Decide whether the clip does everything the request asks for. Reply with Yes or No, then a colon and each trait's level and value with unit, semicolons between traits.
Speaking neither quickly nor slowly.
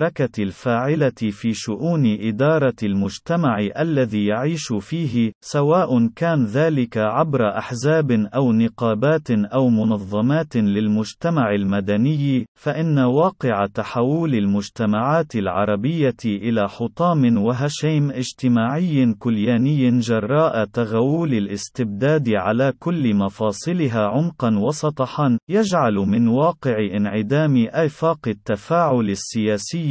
Yes: average, 90 wpm